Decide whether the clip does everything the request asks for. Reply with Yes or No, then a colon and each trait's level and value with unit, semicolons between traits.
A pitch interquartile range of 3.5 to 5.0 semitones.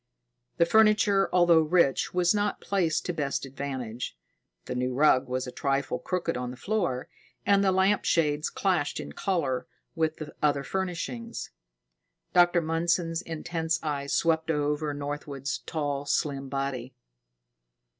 Yes: average, 4.2 semitones